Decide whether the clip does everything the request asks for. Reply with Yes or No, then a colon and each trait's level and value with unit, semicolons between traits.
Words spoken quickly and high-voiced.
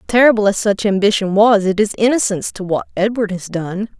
No: average, 195 wpm; high, 205 Hz